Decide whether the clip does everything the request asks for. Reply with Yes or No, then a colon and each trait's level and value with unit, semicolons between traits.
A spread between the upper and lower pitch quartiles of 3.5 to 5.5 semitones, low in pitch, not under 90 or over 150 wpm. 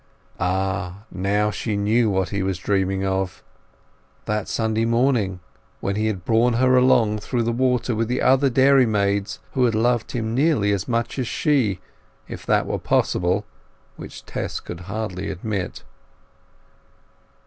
Yes: average, 3.8 semitones; low, 110 Hz; average, 145 wpm